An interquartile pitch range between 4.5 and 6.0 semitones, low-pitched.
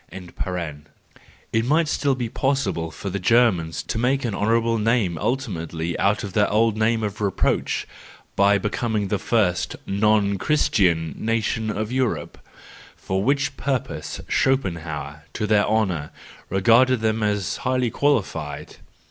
No: average, 4.0 semitones; low, 110 Hz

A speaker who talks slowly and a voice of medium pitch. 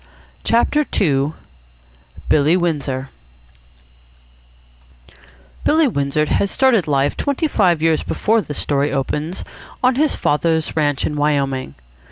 Yes: slow, 110 wpm; medium, 155 Hz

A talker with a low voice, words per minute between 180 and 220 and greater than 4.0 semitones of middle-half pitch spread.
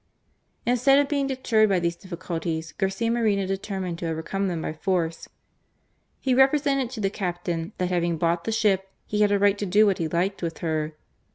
No: high, 195 Hz; average, 190 wpm; average, 4.4 semitones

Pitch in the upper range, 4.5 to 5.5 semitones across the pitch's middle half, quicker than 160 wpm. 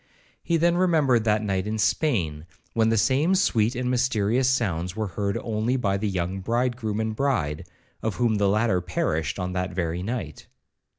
No: low, 110 Hz; average, 5.0 semitones; average, 175 wpm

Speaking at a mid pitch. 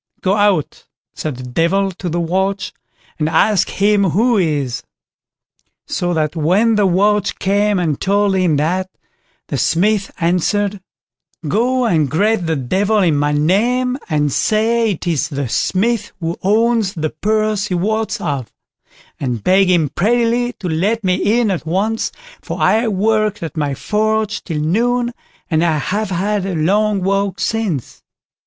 No: high, 195 Hz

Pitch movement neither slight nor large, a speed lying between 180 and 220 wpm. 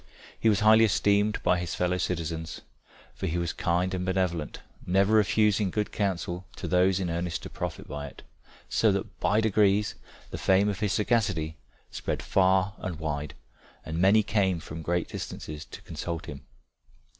No: average, 3.3 semitones; average, 170 wpm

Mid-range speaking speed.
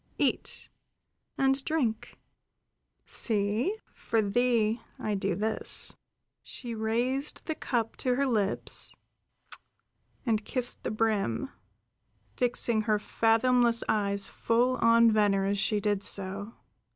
No: slow, 110 wpm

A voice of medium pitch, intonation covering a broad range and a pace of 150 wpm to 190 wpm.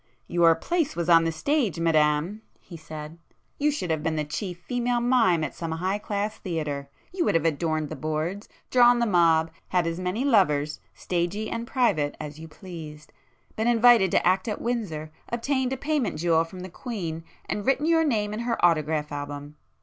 Yes: medium, 175 Hz; wide, 6.7 semitones; average, 180 wpm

